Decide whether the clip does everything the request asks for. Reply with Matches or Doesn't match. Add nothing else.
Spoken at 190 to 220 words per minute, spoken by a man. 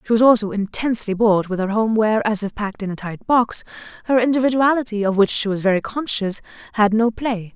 Doesn't match